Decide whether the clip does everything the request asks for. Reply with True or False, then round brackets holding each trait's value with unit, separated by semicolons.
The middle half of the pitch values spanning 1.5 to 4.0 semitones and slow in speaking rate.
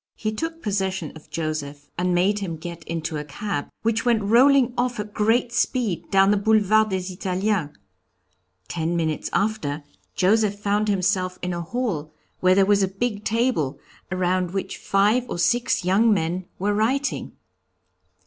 False (3.7 semitones; 160 wpm)